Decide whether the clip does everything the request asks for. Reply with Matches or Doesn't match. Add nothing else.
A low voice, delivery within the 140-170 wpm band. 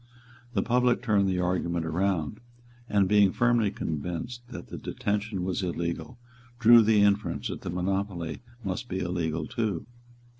Matches